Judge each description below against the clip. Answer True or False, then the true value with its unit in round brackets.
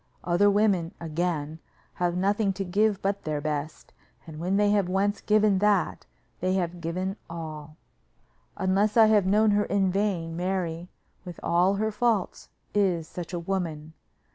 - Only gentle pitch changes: False (3.3 semitones)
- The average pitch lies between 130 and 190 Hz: True (185 Hz)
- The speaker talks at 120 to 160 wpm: True (155 wpm)